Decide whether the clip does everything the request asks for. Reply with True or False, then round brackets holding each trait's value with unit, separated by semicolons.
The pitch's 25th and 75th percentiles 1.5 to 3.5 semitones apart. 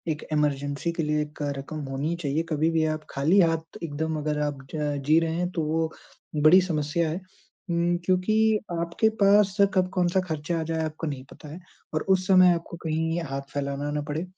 True (2.5 semitones)